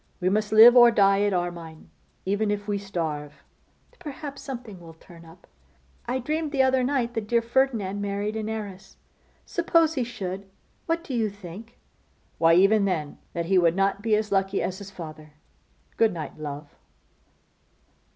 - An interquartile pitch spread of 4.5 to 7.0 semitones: Yes, average, 4.8 semitones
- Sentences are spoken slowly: No, average, 165 wpm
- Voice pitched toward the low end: No, high, 200 Hz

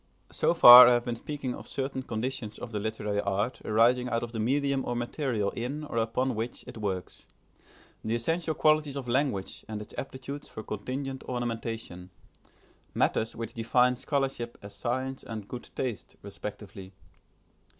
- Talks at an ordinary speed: Yes, average, 160 wpm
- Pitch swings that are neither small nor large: Yes, average, 3.3 semitones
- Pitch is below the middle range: Yes, low, 120 Hz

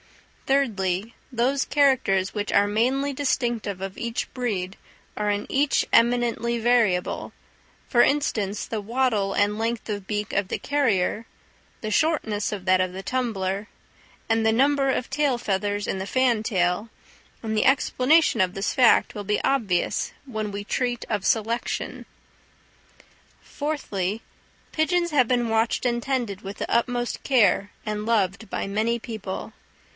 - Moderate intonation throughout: Yes, average, 3.8 semitones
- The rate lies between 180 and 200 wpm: No, average, 145 wpm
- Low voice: No, high, 225 Hz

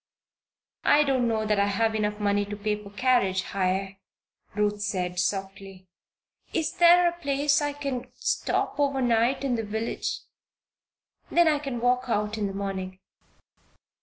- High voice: Yes, high, 220 Hz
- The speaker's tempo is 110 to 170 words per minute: Yes, average, 155 wpm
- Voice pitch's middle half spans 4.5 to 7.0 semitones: Yes, wide, 5.5 semitones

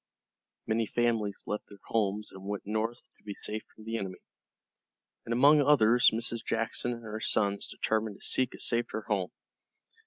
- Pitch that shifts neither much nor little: No, narrow, 2.1 semitones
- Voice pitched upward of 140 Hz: No, low, 110 Hz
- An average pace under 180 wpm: Yes, average, 165 wpm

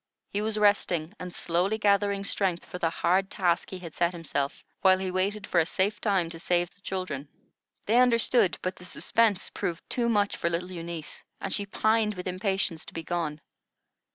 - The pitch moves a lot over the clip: No, average, 2.9 semitones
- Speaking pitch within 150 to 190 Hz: Yes, medium, 185 Hz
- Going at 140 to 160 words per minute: No, average, 190 wpm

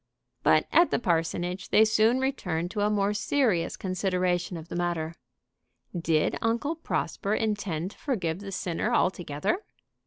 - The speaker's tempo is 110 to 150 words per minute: Yes, average, 145 wpm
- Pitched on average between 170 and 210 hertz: Yes, medium, 185 Hz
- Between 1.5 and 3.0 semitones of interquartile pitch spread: No, average, 4.2 semitones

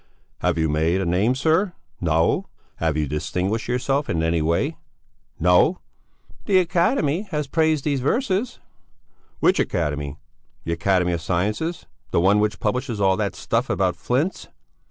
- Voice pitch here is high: No, low, 105 Hz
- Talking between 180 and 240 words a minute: No, average, 145 wpm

